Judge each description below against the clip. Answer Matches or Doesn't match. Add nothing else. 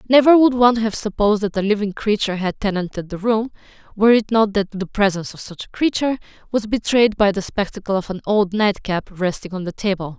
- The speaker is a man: Doesn't match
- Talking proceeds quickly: Matches